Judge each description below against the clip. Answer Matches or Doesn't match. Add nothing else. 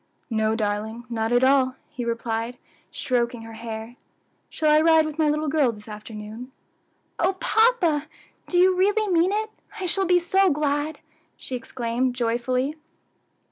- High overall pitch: Matches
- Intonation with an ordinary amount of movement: Doesn't match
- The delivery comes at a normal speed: Matches